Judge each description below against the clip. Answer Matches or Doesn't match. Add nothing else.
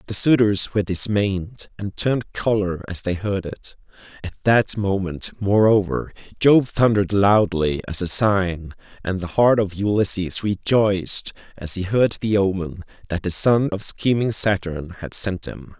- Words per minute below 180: Matches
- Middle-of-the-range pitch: Doesn't match